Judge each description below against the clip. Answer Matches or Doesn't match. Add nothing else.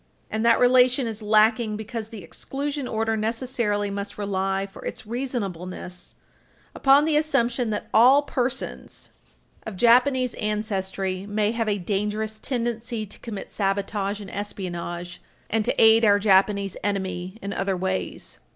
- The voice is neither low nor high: Doesn't match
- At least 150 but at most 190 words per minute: Doesn't match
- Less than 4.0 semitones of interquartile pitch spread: Matches